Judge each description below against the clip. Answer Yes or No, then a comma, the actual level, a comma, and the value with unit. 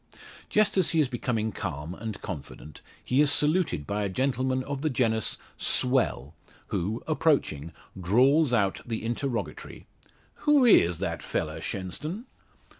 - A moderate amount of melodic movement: No, wide, 7.1 semitones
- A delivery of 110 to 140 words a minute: Yes, slow, 135 wpm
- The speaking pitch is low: Yes, low, 120 Hz